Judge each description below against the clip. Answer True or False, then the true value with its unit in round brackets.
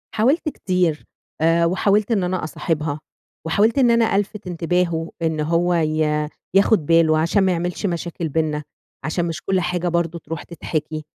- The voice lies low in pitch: False (170 Hz)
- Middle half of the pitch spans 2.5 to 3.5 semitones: True (2.9 semitones)